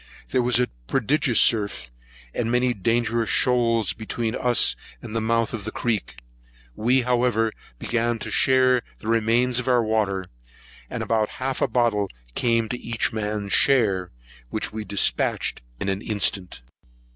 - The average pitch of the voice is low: Yes, low, 115 Hz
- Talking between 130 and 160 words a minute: Yes, average, 150 wpm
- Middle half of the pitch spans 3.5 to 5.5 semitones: No, narrow, 2.4 semitones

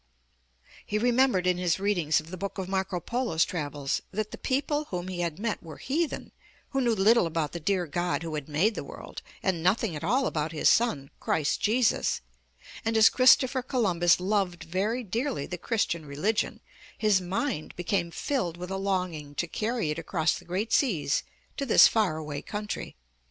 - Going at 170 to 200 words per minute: Yes, average, 185 wpm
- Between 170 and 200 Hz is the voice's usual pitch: Yes, medium, 185 Hz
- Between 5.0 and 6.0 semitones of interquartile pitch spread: Yes, average, 5.3 semitones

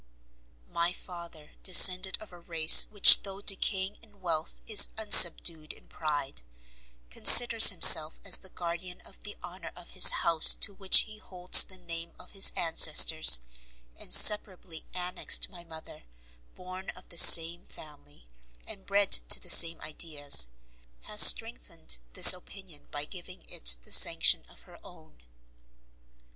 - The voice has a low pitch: No, medium, 175 Hz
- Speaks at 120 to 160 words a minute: Yes, average, 140 wpm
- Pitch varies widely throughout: No, average, 3.0 semitones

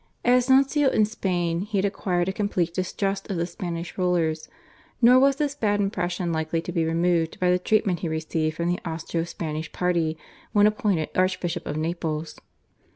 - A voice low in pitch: No, medium, 180 Hz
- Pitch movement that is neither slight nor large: Yes, average, 3.7 semitones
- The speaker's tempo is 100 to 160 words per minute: No, average, 175 wpm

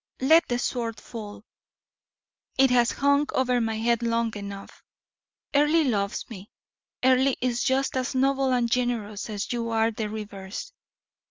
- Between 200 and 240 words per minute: No, average, 145 wpm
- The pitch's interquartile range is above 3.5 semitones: No, average, 3.1 semitones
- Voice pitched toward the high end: Yes, high, 235 Hz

